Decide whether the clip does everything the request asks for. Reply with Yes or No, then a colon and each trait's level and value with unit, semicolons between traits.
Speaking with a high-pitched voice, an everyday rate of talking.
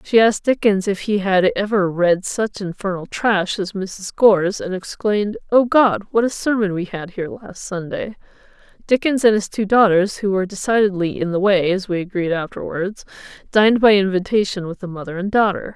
Yes: high, 195 Hz; average, 180 wpm